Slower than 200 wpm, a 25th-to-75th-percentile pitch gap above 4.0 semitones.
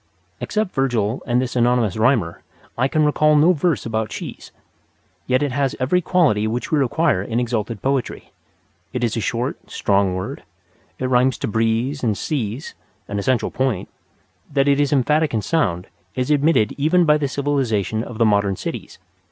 Yes: average, 170 wpm; average, 4.6 semitones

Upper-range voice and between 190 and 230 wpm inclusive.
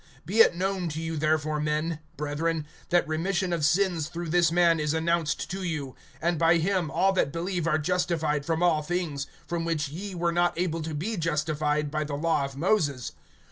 No: medium, 165 Hz; average, 195 wpm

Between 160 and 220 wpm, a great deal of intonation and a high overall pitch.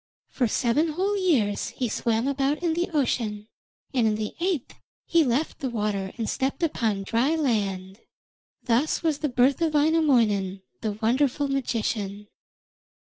No: average, 150 wpm; wide, 6.0 semitones; very high, 250 Hz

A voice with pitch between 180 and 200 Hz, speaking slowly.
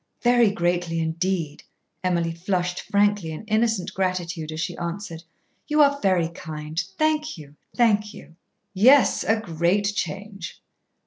Yes: medium, 185 Hz; slow, 130 wpm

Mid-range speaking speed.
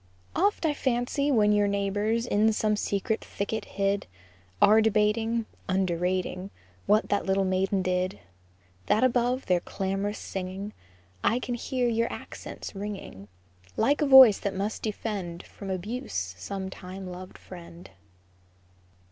No: slow, 130 wpm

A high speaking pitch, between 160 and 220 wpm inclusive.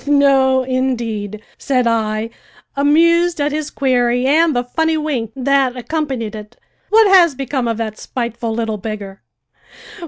No: very high, 255 Hz; slow, 135 wpm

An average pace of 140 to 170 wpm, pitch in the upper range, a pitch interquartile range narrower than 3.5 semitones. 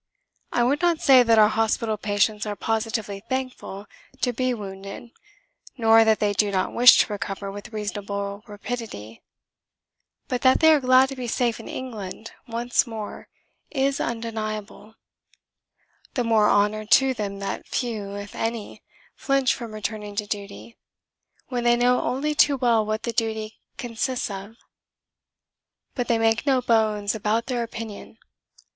Yes: average, 150 wpm; high, 225 Hz; average, 2.9 semitones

